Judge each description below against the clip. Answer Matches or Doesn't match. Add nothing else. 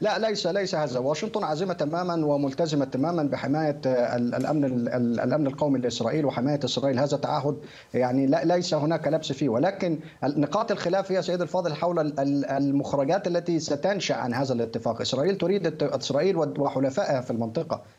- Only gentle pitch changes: Doesn't match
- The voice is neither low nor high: Matches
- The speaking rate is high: Matches